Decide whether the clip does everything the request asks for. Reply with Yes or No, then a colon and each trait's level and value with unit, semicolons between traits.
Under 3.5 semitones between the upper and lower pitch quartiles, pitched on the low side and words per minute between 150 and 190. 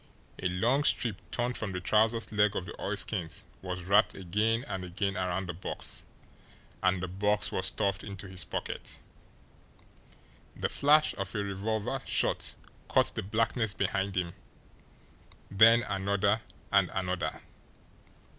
No: average, 3.0 semitones; low, 100 Hz; slow, 135 wpm